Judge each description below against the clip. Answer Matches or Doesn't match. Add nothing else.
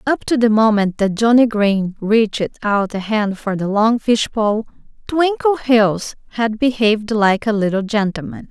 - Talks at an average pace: Matches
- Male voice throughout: Doesn't match